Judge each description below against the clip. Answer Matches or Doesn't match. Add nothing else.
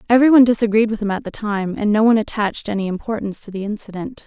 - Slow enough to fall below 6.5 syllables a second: Doesn't match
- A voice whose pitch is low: Doesn't match